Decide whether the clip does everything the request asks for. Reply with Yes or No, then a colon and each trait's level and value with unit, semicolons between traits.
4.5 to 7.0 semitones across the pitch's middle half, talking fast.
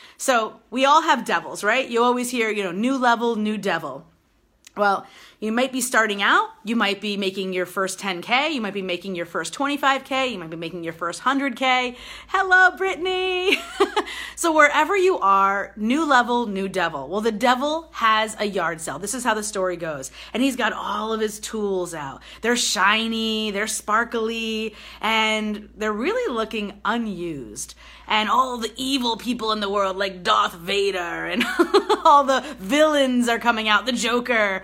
No: average, 4.8 semitones; average, 175 wpm